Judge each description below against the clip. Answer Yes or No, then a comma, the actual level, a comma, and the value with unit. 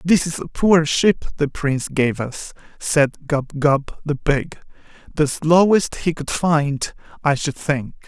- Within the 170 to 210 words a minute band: No, average, 155 wpm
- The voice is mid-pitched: Yes, medium, 150 Hz